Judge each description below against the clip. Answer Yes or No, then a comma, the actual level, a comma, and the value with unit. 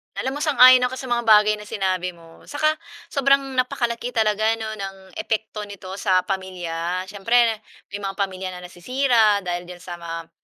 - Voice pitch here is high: Yes, high, 210 Hz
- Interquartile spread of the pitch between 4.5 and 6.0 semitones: Yes, average, 4.8 semitones